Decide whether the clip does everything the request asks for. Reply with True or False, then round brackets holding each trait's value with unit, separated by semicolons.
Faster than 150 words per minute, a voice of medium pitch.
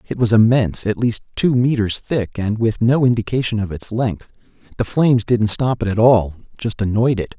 False (205 wpm; 110 Hz)